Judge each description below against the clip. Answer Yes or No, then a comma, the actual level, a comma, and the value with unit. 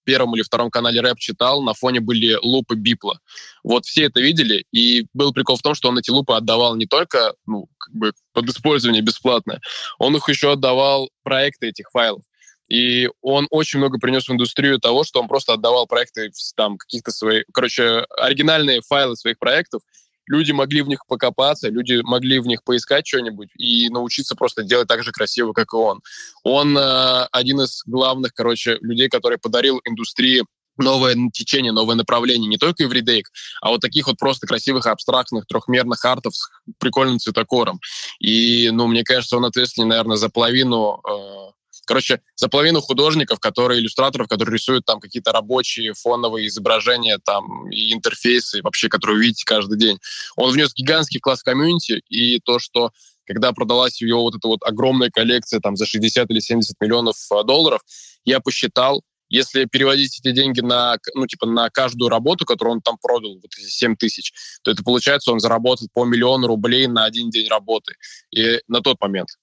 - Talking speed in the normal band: No, fast, 180 wpm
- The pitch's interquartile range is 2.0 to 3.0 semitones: Yes, narrow, 2.4 semitones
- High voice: No, low, 120 Hz